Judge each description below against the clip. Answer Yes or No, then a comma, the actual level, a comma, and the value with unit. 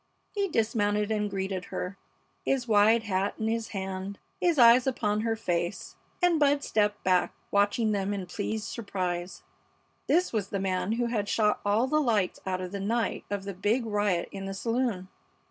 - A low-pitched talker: No, high, 210 Hz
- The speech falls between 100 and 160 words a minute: No, average, 175 wpm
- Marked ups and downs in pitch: No, average, 3.0 semitones